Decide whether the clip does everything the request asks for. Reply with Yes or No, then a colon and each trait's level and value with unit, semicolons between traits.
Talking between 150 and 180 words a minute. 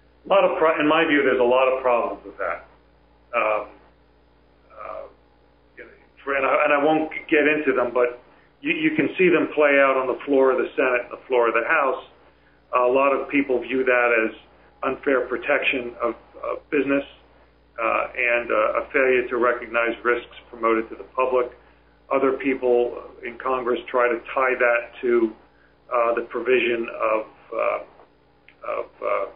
Yes: average, 170 wpm